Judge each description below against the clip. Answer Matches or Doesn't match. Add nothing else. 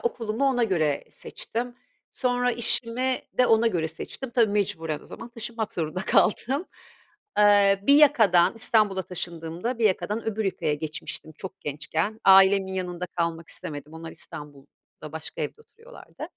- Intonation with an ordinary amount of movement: Doesn't match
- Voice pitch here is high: Matches